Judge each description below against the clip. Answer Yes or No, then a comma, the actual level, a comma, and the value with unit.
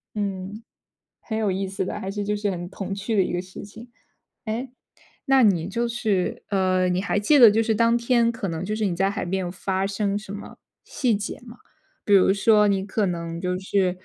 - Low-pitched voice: No, high, 200 Hz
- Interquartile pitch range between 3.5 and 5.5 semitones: No, average, 2.8 semitones